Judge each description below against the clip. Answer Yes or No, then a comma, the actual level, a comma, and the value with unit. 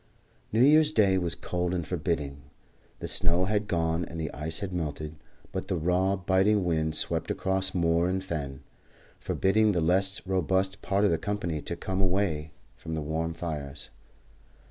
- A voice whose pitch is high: No, very low, 90 Hz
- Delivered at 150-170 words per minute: Yes, average, 165 wpm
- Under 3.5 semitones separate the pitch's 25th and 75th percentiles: Yes, average, 3.1 semitones